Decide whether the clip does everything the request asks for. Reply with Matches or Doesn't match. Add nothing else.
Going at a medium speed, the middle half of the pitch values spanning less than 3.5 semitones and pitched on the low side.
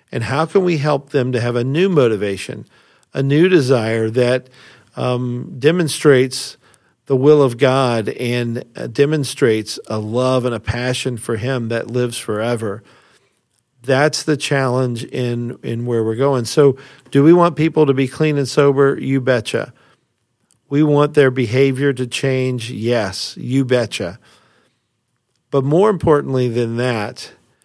Matches